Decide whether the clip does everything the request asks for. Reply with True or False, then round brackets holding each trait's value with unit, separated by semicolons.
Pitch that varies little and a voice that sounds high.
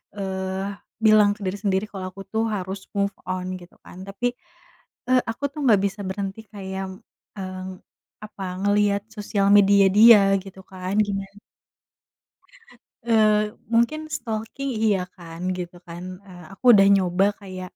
True (1.8 semitones; 200 Hz)